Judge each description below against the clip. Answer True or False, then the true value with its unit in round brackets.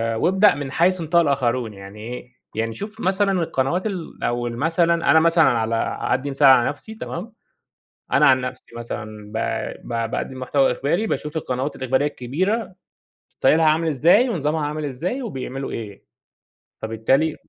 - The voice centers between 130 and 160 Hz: True (140 Hz)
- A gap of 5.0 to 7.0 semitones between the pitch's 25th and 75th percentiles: True (5.5 semitones)